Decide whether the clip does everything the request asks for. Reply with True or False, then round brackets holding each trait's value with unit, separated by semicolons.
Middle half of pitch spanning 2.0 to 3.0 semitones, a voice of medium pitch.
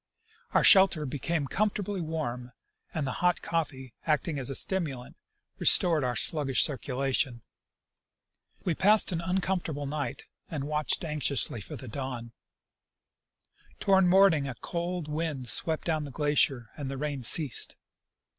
False (4.1 semitones; 150 Hz)